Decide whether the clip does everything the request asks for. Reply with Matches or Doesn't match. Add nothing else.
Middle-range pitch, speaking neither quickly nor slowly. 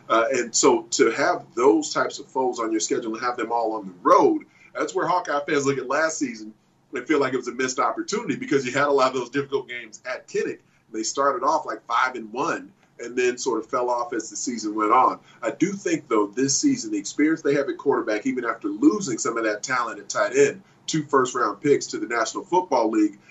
Doesn't match